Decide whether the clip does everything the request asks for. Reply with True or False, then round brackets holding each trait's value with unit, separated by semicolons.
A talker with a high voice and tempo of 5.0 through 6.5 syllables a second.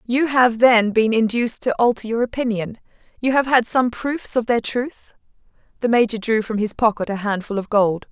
True (230 Hz; 5.1 syllables/s)